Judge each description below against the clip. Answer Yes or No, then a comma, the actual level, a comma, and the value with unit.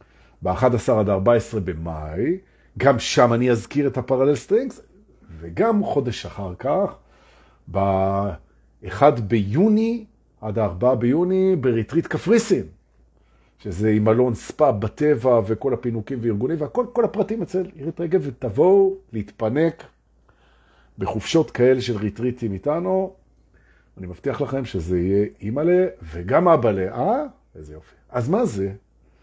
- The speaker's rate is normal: Yes, average, 115 wpm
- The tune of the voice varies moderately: No, wide, 8.0 semitones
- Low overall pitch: Yes, low, 120 Hz